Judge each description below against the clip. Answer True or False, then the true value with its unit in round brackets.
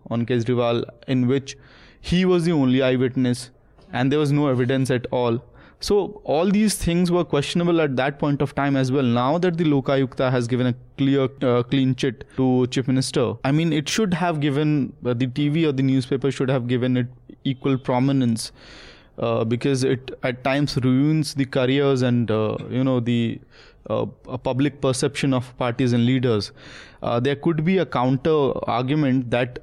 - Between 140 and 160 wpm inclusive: False (180 wpm)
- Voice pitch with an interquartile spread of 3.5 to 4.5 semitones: False (2.4 semitones)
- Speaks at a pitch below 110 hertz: False (135 Hz)